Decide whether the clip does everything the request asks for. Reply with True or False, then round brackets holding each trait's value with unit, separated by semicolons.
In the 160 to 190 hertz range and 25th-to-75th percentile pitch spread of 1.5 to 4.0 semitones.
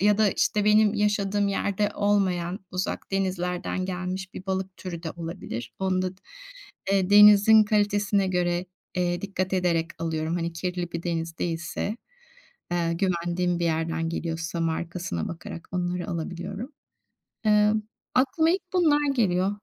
True (185 Hz; 3.1 semitones)